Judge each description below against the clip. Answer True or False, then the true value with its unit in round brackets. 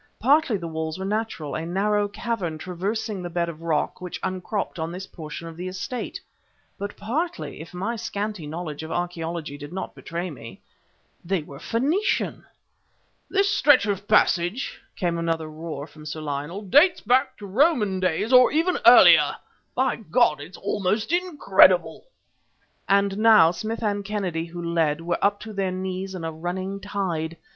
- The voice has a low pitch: False (185 Hz)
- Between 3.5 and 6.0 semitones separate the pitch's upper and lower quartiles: True (4.3 semitones)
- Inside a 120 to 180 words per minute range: True (165 wpm)